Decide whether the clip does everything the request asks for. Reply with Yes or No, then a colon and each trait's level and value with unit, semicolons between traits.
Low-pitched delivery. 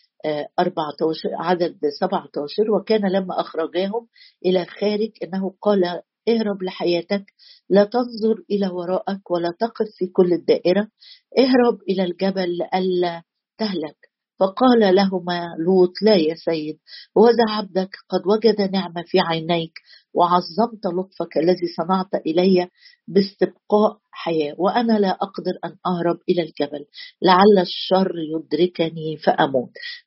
No: medium, 185 Hz